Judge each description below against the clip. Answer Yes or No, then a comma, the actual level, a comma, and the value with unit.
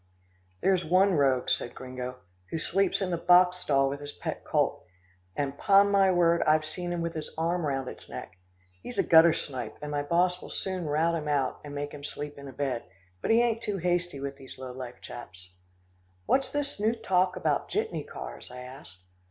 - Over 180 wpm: Yes, average, 200 wpm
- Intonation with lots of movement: No, average, 4.9 semitones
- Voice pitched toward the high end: No, medium, 155 Hz